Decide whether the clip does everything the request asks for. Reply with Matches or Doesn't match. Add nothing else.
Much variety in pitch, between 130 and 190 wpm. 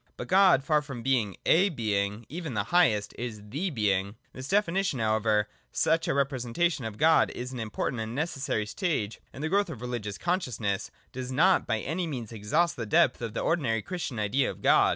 Doesn't match